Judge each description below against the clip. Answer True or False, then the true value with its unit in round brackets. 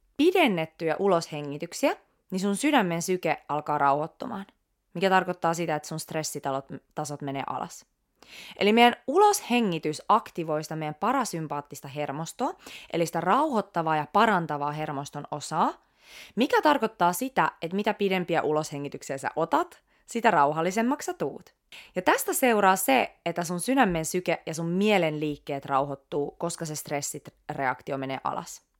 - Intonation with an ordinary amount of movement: False (5.9 semitones)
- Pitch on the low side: False (170 Hz)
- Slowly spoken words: True (130 wpm)